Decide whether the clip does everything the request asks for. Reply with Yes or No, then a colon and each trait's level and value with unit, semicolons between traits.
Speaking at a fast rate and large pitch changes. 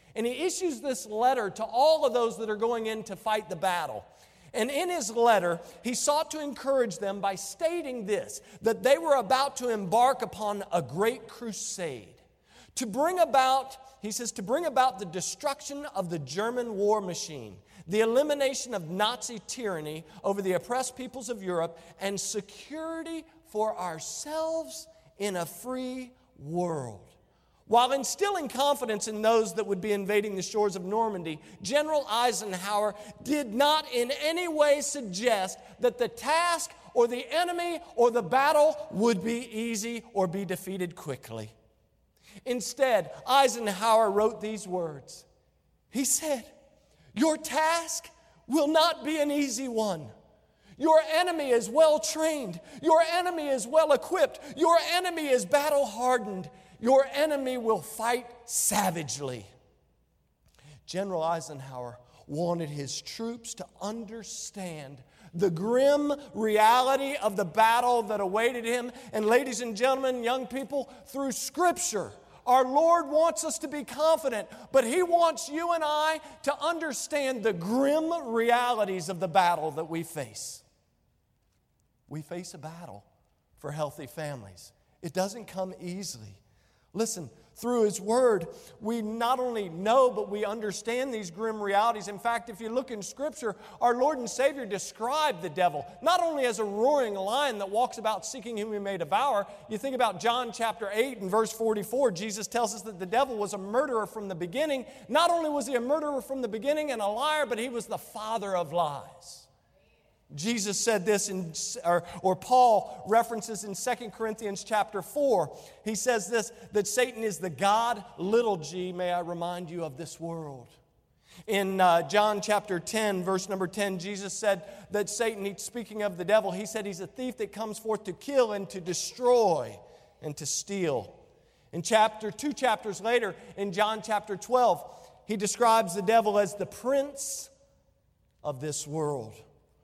No: average, 155 wpm; wide, 5.7 semitones